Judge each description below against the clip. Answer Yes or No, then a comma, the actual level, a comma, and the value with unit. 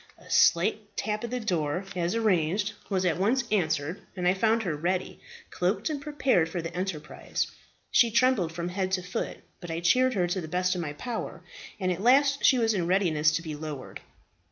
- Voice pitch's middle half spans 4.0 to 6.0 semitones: Yes, average, 4.8 semitones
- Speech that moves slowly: No, average, 200 wpm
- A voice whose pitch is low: No, medium, 185 Hz